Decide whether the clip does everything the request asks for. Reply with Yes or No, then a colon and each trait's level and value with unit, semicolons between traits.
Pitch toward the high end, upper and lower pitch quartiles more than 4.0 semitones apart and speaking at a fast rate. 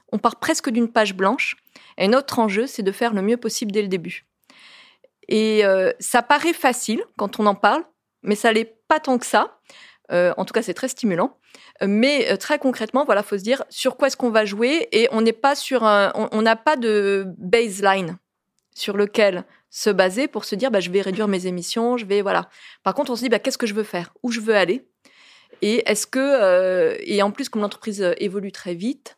Yes: high, 225 Hz; average, 4.5 semitones; fast, 225 wpm